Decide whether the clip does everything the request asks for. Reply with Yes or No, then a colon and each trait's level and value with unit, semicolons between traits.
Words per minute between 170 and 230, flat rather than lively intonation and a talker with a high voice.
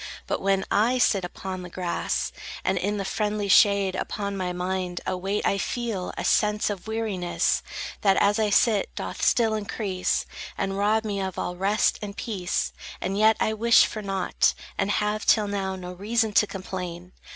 Yes: average, 180 wpm; narrow, 2.2 semitones; high, 200 Hz